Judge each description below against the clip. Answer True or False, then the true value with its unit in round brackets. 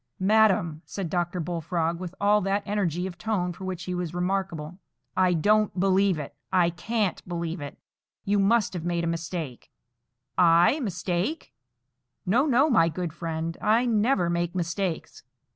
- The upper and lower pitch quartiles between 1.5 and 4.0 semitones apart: True (3.0 semitones)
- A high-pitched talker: False (180 Hz)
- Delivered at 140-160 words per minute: True (150 wpm)